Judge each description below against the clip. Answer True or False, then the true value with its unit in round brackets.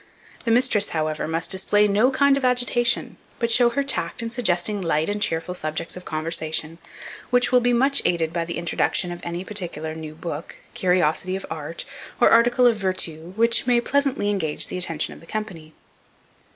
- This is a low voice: False (185 Hz)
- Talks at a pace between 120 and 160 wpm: False (180 wpm)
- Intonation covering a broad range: True (6.3 semitones)